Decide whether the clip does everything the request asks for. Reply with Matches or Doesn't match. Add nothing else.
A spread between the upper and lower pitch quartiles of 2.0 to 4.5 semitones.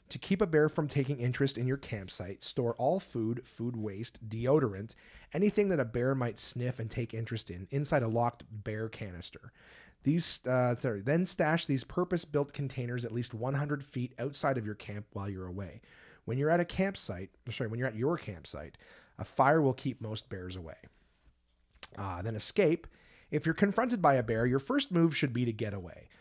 Doesn't match